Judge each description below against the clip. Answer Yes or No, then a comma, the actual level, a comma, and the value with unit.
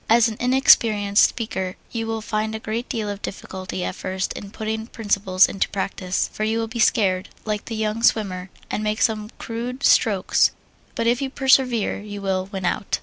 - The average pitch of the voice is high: Yes, high, 215 Hz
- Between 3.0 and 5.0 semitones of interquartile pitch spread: No, narrow, 2.5 semitones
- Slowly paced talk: No, average, 190 wpm